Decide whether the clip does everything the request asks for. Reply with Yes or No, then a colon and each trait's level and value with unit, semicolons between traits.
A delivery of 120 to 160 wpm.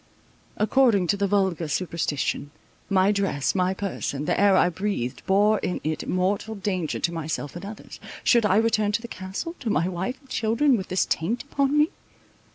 No: average, 180 wpm